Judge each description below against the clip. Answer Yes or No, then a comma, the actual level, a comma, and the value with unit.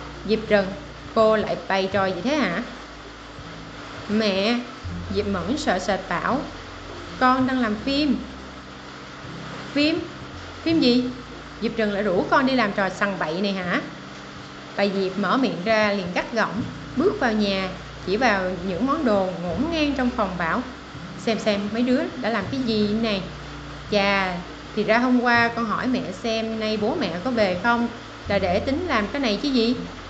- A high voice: Yes, high, 215 Hz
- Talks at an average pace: Yes, average, 175 wpm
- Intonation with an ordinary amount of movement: Yes, average, 4.5 semitones